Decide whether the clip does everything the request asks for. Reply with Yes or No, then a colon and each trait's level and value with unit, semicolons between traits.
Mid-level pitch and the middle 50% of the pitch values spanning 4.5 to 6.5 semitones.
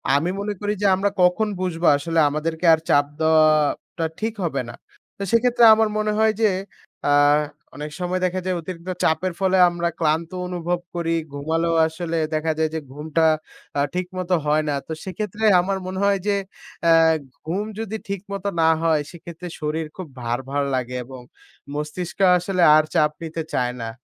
No: medium, 170 Hz; average, 3.3 semitones